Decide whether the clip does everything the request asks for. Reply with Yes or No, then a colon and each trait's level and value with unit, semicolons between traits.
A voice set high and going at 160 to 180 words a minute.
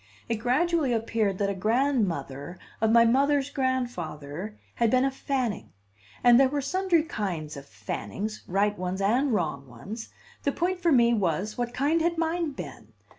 Yes: high, 230 Hz; average, 165 wpm